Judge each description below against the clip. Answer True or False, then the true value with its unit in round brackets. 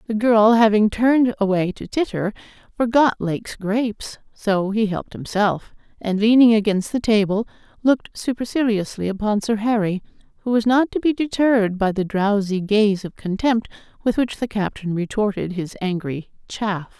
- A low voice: False (215 Hz)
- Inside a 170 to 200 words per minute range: False (155 wpm)